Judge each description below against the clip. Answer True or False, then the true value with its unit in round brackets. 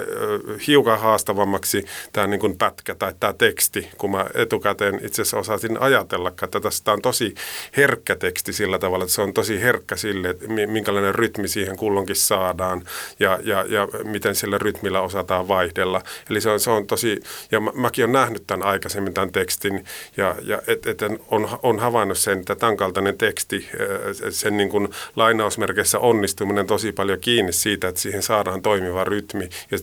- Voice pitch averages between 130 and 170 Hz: False (100 Hz)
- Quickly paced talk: True (165 wpm)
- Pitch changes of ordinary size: False (2.2 semitones)